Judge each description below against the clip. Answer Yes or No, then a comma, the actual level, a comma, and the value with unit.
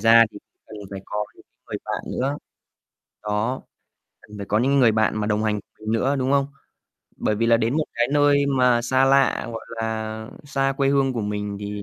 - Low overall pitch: Yes, low, 115 Hz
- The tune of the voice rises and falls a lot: No, average, 4.1 semitones